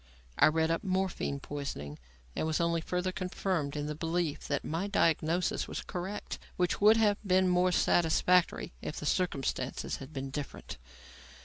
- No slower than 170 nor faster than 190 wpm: No, average, 155 wpm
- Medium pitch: Yes, medium, 170 Hz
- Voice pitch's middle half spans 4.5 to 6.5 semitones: No, average, 3.7 semitones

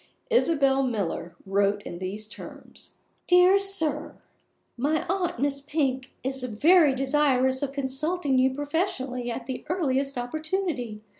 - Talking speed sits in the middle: No, slow, 125 wpm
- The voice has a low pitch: No, very high, 270 Hz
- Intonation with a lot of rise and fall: No, average, 3.9 semitones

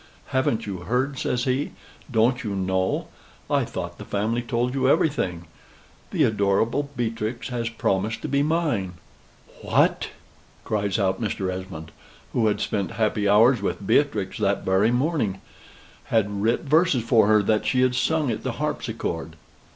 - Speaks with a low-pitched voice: Yes, low, 110 Hz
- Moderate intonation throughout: Yes, average, 4.3 semitones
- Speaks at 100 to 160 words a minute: Yes, average, 150 wpm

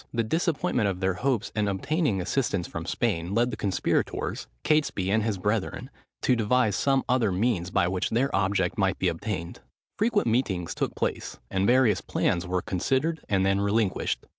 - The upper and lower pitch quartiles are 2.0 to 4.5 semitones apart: No, average, 5.1 semitones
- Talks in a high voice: No, low, 105 Hz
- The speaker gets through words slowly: No, average, 170 wpm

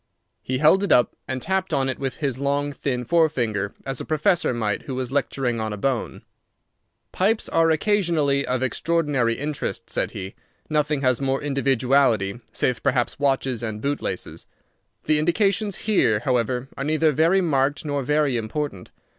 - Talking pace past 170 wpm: No, average, 165 wpm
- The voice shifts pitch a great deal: No, average, 3.8 semitones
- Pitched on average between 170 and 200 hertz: No, medium, 140 Hz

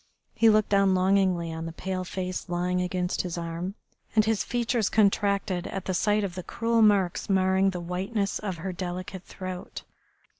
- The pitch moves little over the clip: Yes, narrow, 2.0 semitones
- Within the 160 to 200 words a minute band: Yes, average, 175 wpm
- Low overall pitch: No, high, 190 Hz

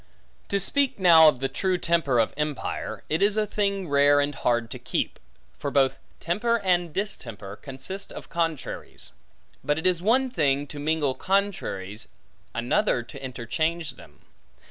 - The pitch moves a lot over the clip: Yes, wide, 6.2 semitones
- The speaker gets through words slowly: No, average, 155 wpm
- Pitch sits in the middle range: Yes, medium, 155 Hz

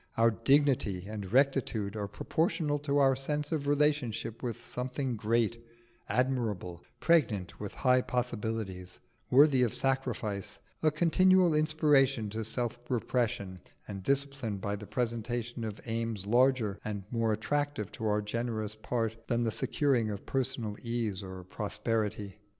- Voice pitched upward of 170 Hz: No, low, 115 Hz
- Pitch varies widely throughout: No, average, 4.3 semitones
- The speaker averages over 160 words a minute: No, slow, 135 wpm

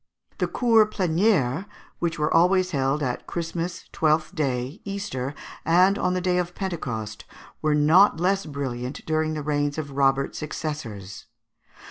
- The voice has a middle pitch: Yes, medium, 155 Hz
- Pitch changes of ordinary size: Yes, average, 4.7 semitones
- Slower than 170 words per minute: Yes, average, 140 wpm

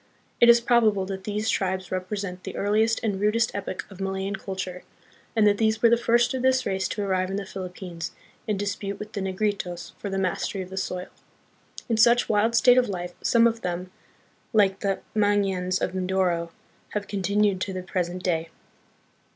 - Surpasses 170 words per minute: Yes, average, 190 wpm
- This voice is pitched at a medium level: No, high, 195 Hz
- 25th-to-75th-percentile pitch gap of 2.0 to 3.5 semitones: Yes, narrow, 2.6 semitones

